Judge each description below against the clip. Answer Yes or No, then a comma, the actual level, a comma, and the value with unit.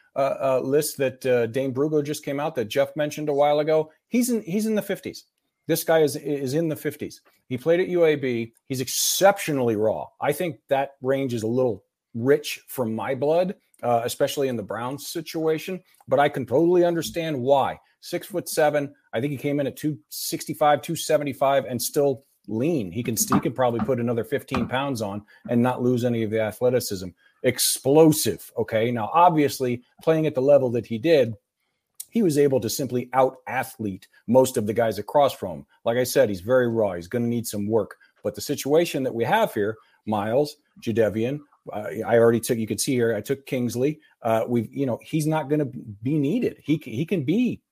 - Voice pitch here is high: No, low, 135 Hz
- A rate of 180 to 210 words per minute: Yes, average, 200 wpm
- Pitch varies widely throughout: No, average, 4.2 semitones